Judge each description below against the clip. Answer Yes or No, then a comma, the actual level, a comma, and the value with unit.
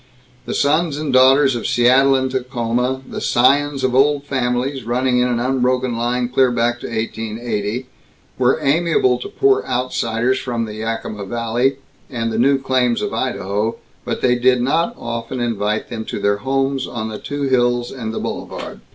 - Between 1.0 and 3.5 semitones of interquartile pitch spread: Yes, narrow, 2.4 semitones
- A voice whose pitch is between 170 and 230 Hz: No, low, 125 Hz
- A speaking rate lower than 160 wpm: No, average, 170 wpm